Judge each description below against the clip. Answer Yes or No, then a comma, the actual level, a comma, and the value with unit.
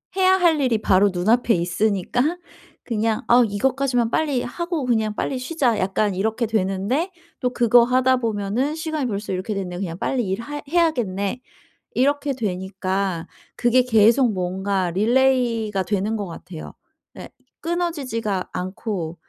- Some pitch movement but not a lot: Yes, average, 5.0 semitones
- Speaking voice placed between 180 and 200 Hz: No, high, 225 Hz